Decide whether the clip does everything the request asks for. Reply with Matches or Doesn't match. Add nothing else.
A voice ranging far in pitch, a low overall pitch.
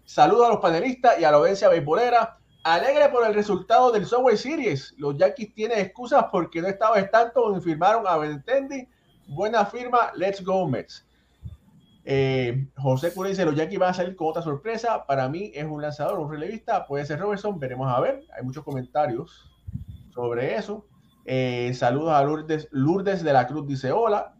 Doesn't match